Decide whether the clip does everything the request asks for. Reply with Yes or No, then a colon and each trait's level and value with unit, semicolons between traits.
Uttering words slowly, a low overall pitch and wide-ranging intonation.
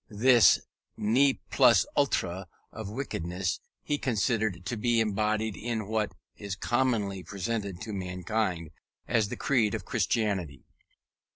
No: slow, 120 wpm; low, 105 Hz; average, 3.4 semitones